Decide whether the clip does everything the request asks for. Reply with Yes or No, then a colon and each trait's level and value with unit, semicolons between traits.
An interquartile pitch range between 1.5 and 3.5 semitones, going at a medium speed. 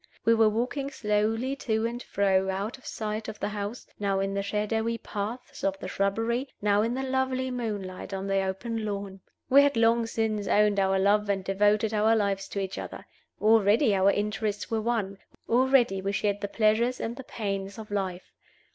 Yes: narrow, 2.5 semitones; average, 190 wpm